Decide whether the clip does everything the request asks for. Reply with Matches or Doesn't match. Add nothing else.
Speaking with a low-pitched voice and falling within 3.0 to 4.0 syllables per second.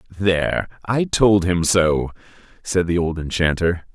Matches